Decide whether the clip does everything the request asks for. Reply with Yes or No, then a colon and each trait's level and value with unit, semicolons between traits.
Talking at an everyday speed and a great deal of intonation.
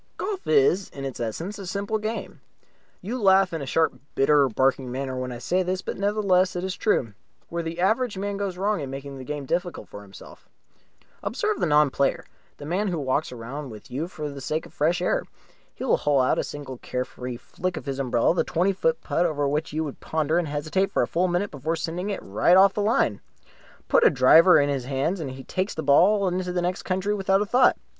No: fast, 235 wpm; wide, 5.7 semitones